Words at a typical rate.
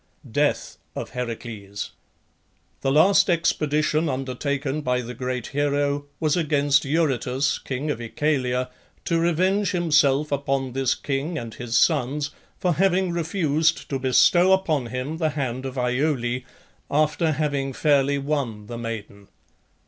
No: slow, 130 wpm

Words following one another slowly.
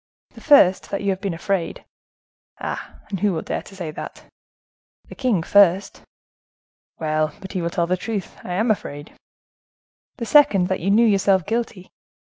No: average, 165 wpm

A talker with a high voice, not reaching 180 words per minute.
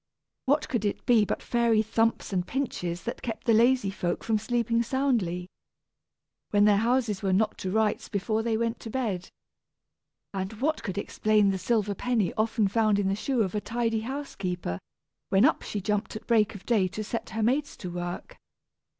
No: high, 215 Hz; average, 185 wpm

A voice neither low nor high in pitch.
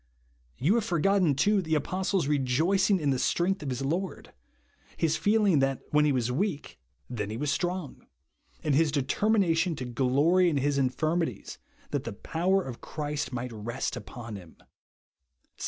Yes: medium, 150 Hz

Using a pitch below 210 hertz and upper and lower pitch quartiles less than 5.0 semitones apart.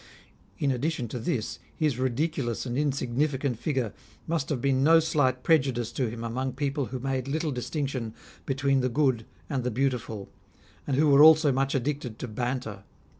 Yes: low, 135 Hz; average, 2.9 semitones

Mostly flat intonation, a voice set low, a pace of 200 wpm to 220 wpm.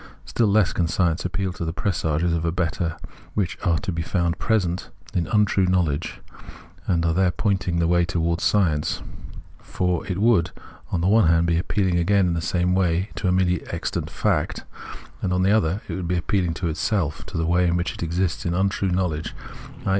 Yes: narrow, 2.2 semitones; very low, 90 Hz; fast, 205 wpm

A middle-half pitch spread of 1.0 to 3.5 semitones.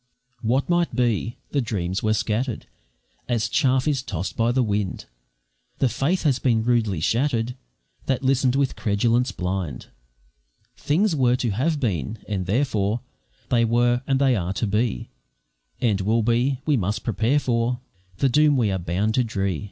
No: average, 4.0 semitones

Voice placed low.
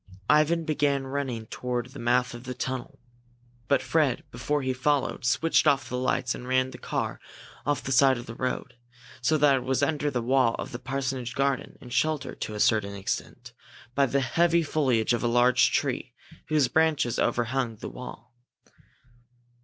Yes: low, 130 Hz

